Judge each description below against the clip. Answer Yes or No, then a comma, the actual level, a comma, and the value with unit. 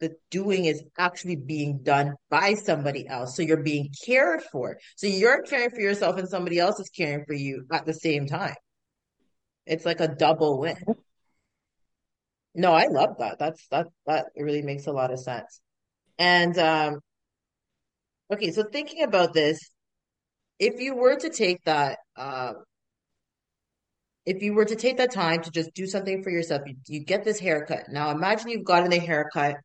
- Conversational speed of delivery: Yes, average, 175 wpm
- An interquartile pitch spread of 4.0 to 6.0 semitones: Yes, average, 4.6 semitones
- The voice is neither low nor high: Yes, medium, 165 Hz